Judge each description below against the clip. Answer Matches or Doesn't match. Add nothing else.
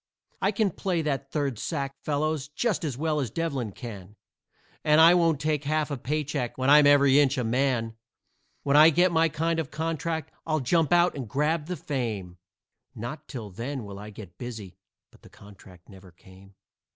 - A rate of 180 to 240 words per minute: Matches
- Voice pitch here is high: Doesn't match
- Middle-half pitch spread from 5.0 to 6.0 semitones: Matches